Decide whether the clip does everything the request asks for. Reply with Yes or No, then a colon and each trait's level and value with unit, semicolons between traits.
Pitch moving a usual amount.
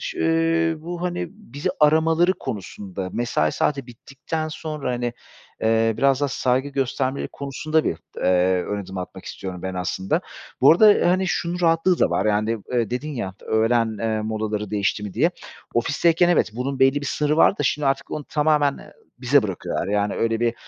No: wide, 6.4 semitones